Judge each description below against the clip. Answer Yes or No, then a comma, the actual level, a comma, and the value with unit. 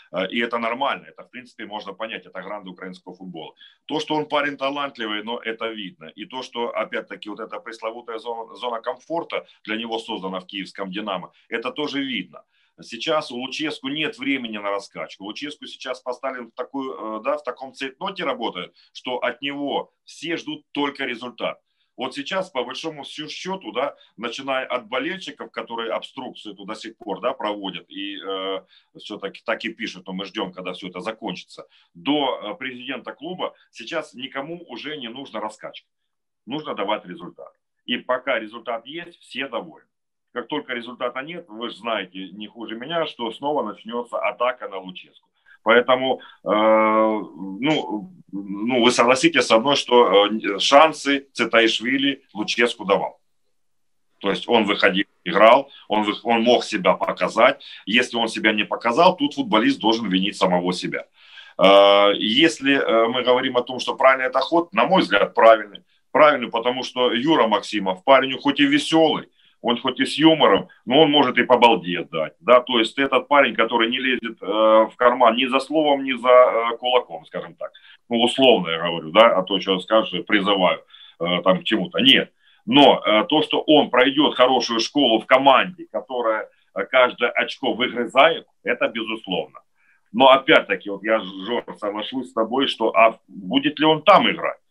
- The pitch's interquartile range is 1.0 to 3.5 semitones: No, average, 4.4 semitones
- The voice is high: No, low, 120 Hz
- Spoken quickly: Yes, fast, 165 wpm